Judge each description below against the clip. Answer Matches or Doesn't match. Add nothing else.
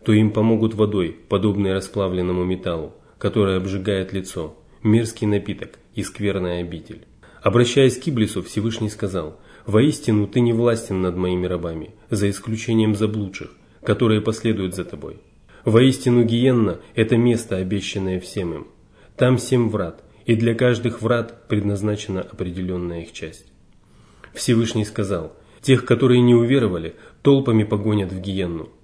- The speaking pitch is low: Matches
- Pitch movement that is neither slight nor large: Matches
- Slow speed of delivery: Doesn't match